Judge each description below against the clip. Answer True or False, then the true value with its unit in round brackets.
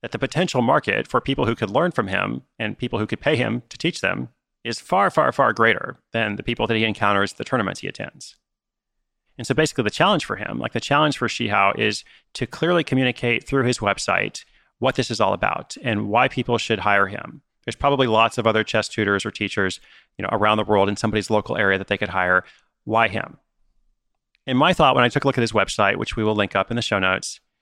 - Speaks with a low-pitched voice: True (110 Hz)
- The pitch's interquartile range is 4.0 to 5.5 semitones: False (3.5 semitones)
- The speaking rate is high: True (240 wpm)